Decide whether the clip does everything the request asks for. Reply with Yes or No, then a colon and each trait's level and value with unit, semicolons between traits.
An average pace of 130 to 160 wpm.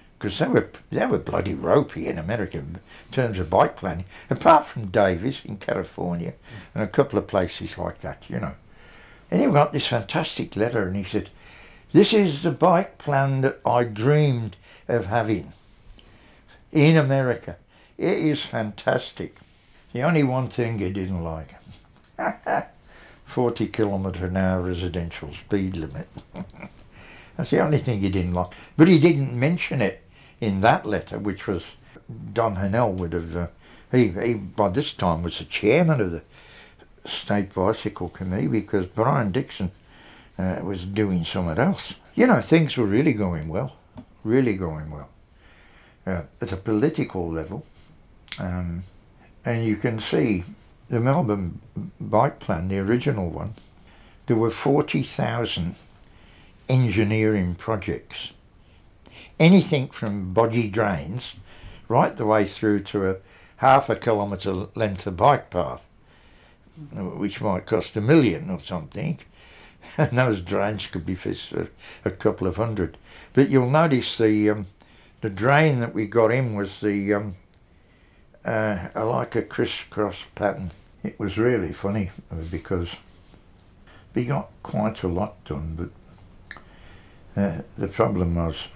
Yes: average, 140 wpm